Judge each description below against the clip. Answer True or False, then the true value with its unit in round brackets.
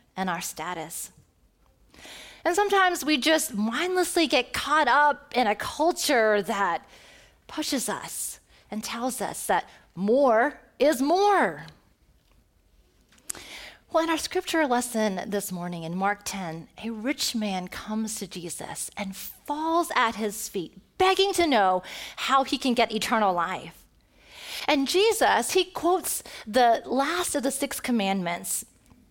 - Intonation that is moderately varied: False (8.1 semitones)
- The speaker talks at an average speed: False (130 wpm)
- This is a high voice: True (255 Hz)